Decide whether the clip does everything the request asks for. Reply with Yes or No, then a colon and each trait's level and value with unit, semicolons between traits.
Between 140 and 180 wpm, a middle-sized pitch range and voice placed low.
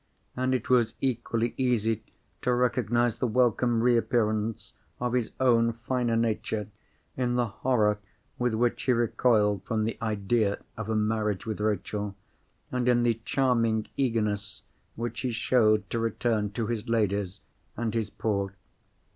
No: average, 145 wpm; narrow, 2.3 semitones; low, 115 Hz